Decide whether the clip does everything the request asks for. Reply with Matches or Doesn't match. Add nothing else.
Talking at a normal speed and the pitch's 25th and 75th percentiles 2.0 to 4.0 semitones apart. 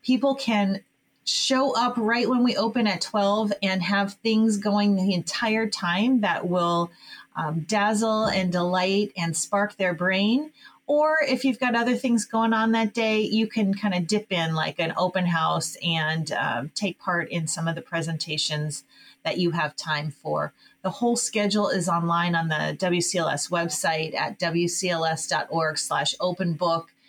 Doesn't match